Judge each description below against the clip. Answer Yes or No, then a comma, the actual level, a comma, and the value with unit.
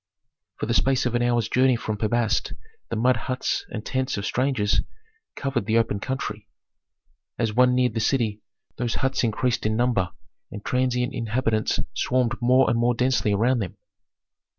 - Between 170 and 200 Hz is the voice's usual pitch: No, low, 120 Hz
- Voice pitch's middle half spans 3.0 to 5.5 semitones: No, narrow, 2.5 semitones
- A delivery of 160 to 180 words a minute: Yes, average, 170 wpm